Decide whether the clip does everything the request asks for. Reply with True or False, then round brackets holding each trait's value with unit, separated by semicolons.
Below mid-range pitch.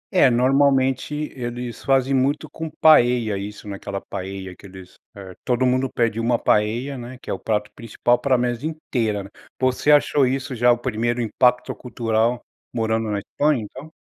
True (120 Hz)